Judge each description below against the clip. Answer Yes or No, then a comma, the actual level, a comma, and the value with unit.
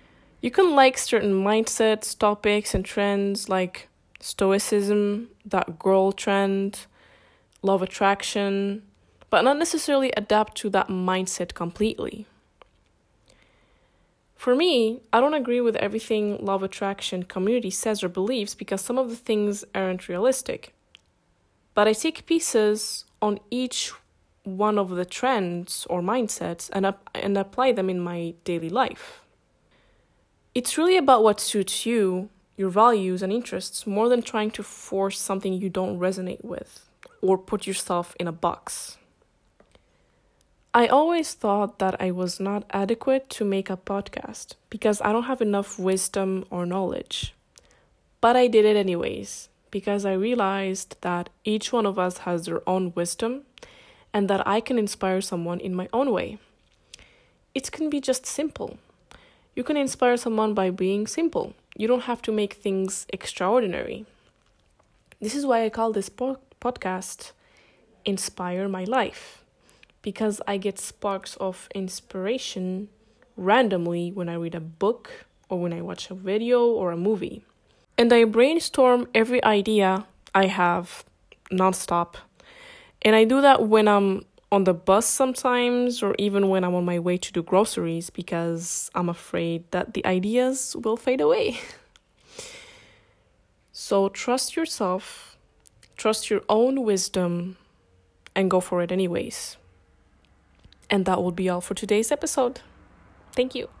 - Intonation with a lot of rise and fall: No, average, 3.9 semitones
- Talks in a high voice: Yes, high, 200 Hz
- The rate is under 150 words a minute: Yes, average, 140 wpm